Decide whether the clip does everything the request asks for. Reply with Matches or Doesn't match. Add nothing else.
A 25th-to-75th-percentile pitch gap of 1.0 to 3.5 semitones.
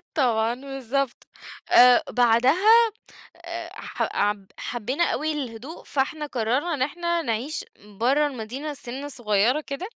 Doesn't match